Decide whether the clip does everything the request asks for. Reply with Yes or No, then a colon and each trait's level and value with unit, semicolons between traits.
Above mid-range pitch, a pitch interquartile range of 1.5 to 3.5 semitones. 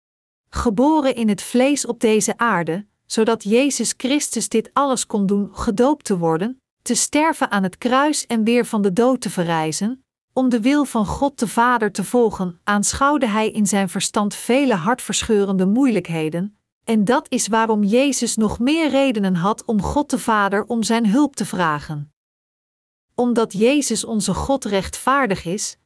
No: high, 225 Hz; average, 4.0 semitones